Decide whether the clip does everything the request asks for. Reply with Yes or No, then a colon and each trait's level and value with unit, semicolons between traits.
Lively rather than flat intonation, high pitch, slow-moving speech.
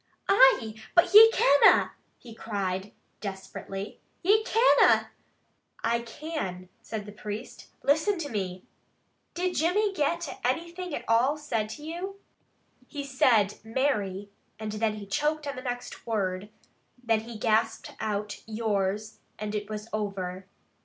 Yes: wide, 6.2 semitones; high, 225 Hz; slow, 130 wpm